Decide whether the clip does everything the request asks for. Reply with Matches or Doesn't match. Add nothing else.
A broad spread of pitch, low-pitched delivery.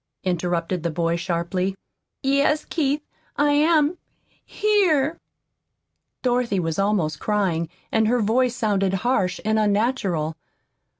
Doesn't match